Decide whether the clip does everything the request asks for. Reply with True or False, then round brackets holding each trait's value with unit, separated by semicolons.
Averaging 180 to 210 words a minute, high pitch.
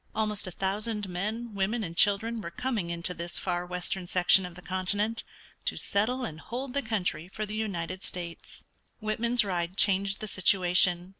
False (170 wpm; 195 Hz)